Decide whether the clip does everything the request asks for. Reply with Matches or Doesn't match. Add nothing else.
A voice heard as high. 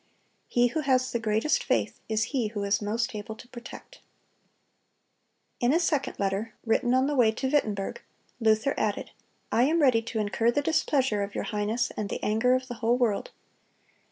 Matches